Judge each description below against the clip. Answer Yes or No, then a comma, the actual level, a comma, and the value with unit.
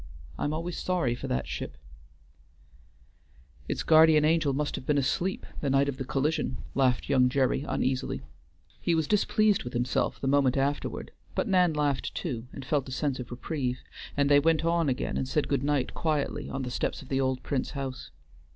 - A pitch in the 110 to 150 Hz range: Yes, medium, 140 Hz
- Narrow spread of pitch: No, average, 3.1 semitones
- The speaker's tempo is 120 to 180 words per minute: No, average, 190 wpm